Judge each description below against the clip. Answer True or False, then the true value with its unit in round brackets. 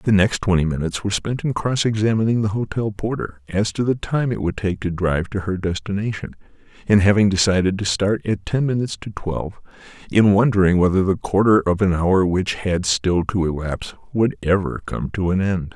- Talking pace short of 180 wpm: False (200 wpm)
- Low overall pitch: True (100 Hz)